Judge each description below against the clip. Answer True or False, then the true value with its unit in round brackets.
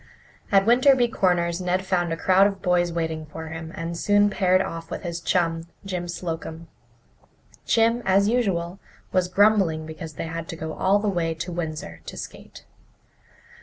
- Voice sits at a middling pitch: True (175 Hz)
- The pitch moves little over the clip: False (3.0 semitones)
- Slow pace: False (165 wpm)